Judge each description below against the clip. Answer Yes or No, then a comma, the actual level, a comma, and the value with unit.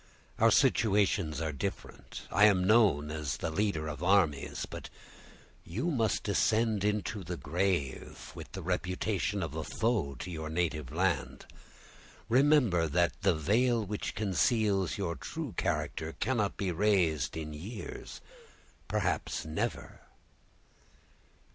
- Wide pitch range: No, average, 5.0 semitones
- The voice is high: No, very low, 95 Hz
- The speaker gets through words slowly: Yes, slow, 120 wpm